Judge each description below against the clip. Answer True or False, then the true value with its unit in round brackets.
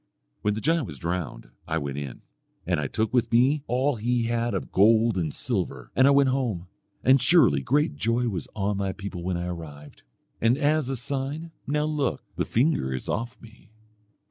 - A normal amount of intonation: False (7.1 semitones)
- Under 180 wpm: False (195 wpm)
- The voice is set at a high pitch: False (115 Hz)